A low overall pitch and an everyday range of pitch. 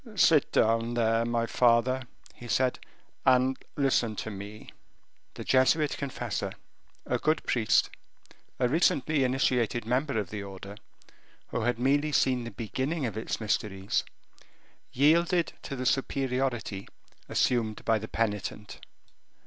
Yes: low, 120 Hz; average, 3.4 semitones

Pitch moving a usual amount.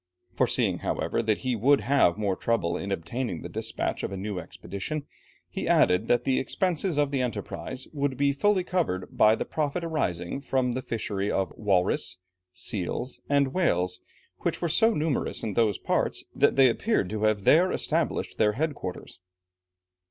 No: wide, 6.7 semitones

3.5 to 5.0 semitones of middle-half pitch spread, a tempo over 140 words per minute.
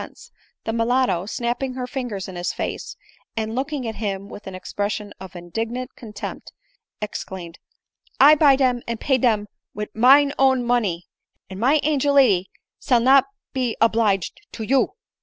Yes: average, 4.3 semitones; average, 170 wpm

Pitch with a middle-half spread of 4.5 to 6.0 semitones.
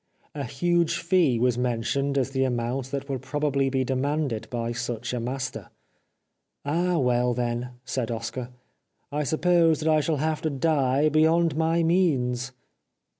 No: average, 4.1 semitones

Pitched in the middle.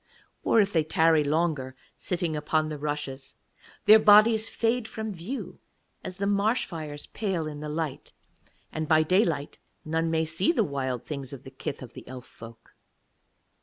Yes: medium, 160 Hz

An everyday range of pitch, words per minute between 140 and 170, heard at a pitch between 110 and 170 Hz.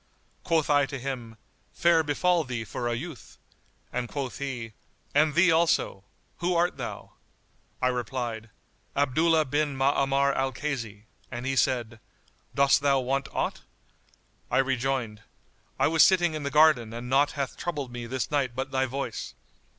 Yes: average, 3.4 semitones; average, 155 wpm; low, 135 Hz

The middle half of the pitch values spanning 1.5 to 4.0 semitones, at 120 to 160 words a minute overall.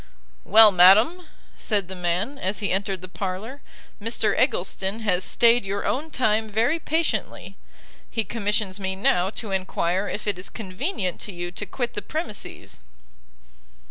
Yes: average, 3.4 semitones; average, 150 wpm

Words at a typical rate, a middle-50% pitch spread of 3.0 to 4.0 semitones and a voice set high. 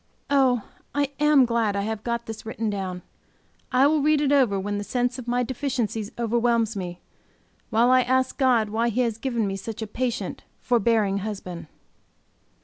Yes: average, 175 wpm; average, 3.3 semitones; high, 235 Hz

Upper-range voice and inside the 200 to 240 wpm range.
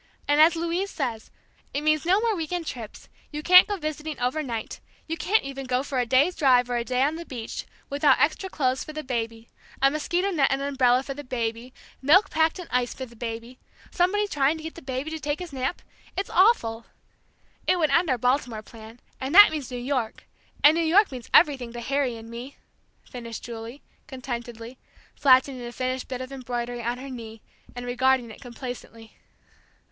Yes: very high, 265 Hz; fast, 205 wpm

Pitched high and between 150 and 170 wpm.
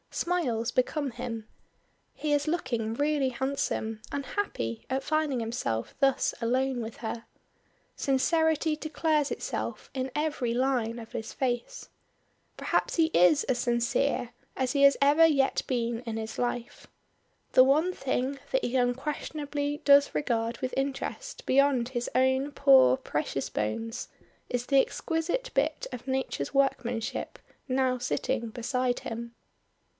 No: very high, 260 Hz; slow, 135 wpm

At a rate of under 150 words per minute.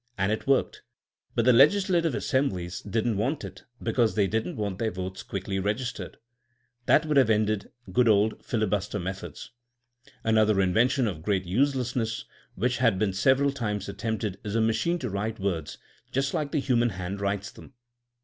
No: average, 165 wpm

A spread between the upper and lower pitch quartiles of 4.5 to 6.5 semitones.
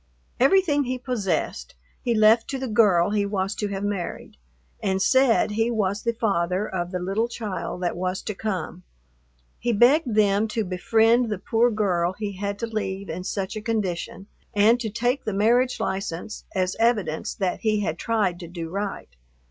No: average, 3.5 semitones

